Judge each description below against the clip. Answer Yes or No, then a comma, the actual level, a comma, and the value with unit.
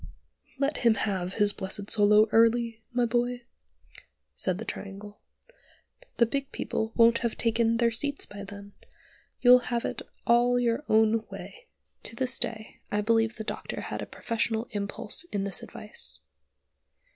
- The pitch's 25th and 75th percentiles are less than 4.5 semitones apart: Yes, narrow, 2.6 semitones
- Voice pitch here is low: No, high, 225 Hz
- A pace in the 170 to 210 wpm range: No, average, 150 wpm